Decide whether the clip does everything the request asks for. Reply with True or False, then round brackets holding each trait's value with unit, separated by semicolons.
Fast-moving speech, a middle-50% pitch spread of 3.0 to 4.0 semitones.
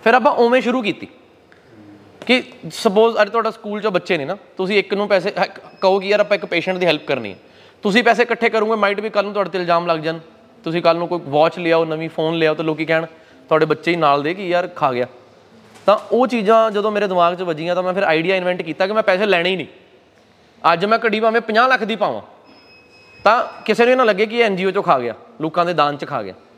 False (245 wpm; 5.1 semitones)